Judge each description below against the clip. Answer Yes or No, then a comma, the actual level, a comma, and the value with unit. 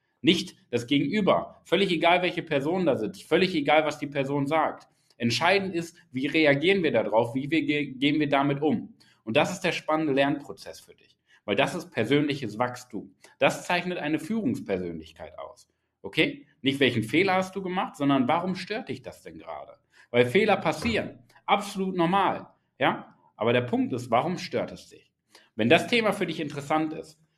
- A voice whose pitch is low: No, medium, 155 Hz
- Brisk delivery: No, average, 175 wpm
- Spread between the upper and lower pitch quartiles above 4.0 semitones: Yes, average, 4.5 semitones